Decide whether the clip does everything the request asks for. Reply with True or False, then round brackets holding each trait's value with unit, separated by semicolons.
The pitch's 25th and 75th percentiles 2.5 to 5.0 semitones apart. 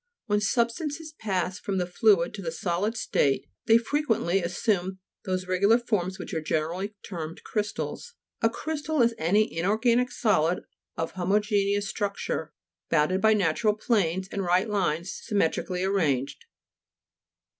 True (3.9 semitones)